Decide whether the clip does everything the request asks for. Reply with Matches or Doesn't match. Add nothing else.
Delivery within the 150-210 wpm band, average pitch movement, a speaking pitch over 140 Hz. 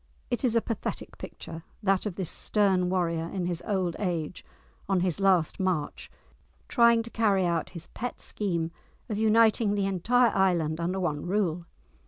Matches